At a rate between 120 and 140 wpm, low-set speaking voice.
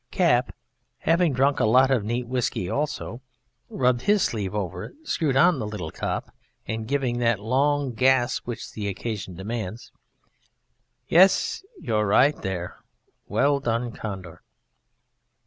Yes: slow, 135 wpm; low, 120 Hz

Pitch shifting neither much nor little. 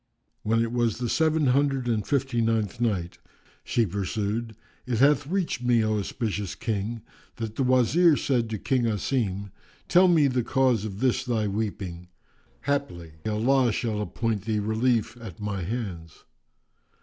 Yes: average, 3.6 semitones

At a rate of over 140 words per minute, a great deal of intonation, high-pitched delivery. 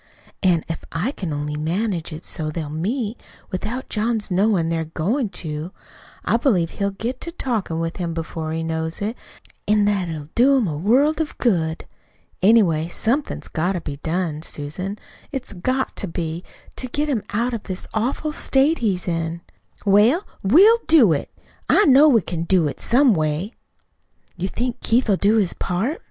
Yes: average, 175 wpm; wide, 6.6 semitones; high, 195 Hz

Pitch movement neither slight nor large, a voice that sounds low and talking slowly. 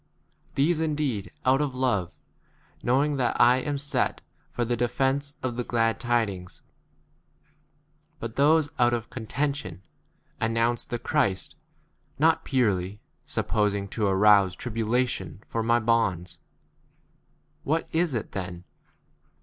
Yes: average, 4.7 semitones; low, 120 Hz; slow, 130 wpm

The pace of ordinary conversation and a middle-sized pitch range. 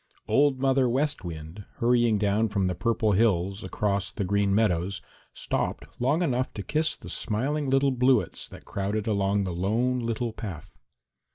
Yes: average, 160 wpm; average, 4.4 semitones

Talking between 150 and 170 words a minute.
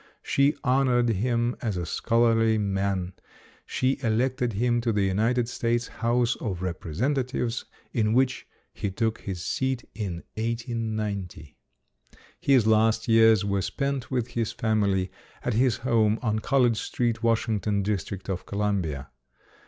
No: slow, 135 wpm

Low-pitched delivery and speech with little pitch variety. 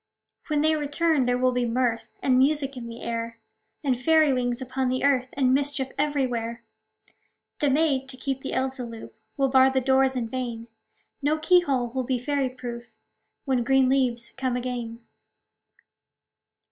No: very high, 260 Hz; narrow, 2.0 semitones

